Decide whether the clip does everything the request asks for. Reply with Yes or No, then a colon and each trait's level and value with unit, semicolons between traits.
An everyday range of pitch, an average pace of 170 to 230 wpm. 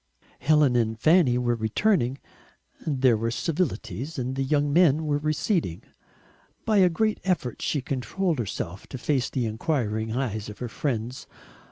No: average, 5.0 semitones; average, 150 wpm